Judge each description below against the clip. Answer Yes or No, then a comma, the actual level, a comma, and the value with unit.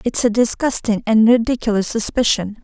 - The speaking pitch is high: Yes, high, 225 Hz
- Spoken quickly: No, slow, 135 wpm